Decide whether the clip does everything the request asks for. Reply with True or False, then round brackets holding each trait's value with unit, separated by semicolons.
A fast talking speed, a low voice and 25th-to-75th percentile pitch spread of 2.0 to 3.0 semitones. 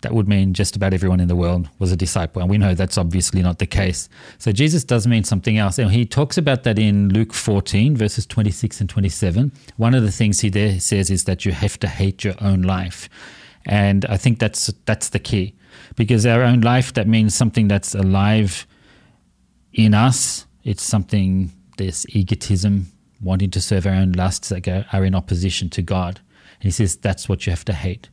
True (210 wpm; 100 Hz; 2.7 semitones)